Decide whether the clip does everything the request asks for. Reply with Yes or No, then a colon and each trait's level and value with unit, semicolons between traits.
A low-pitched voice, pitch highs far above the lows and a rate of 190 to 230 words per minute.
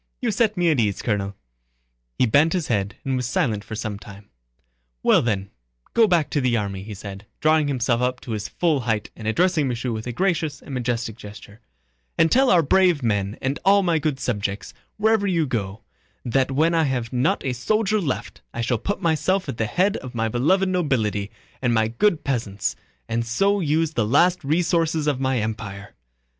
Yes: low, 130 Hz; wide, 6.9 semitones; average, 195 wpm